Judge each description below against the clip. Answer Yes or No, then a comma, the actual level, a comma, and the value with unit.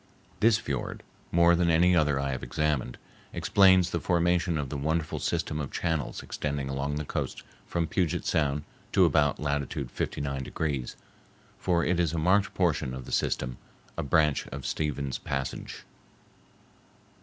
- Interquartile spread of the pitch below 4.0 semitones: Yes, average, 3.6 semitones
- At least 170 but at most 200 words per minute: No, average, 150 wpm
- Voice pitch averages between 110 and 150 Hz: No, very low, 75 Hz